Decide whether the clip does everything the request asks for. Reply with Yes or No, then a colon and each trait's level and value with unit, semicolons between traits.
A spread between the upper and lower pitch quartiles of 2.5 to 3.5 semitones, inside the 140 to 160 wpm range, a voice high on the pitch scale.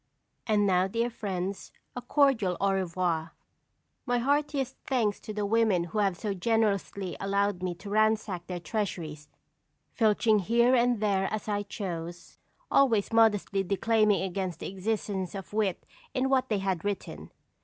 Yes: average, 3.2 semitones; average, 150 wpm; high, 205 Hz